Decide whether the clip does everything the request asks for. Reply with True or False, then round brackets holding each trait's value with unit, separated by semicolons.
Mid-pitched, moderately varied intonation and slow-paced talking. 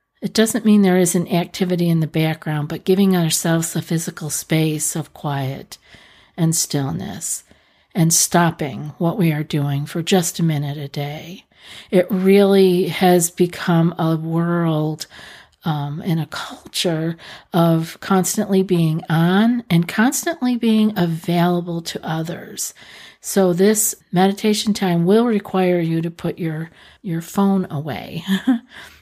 True (175 Hz; 3.0 semitones; 130 wpm)